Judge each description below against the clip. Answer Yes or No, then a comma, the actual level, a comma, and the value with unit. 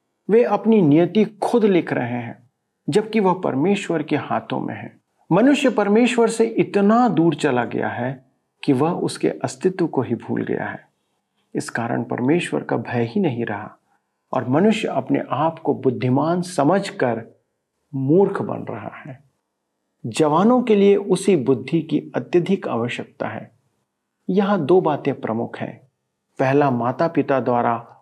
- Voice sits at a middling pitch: Yes, medium, 165 Hz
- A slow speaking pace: No, average, 145 wpm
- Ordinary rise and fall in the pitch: No, wide, 7.4 semitones